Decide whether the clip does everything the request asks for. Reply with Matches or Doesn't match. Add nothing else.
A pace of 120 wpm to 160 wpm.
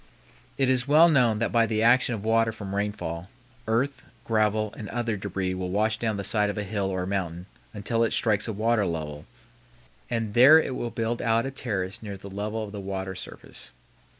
Doesn't match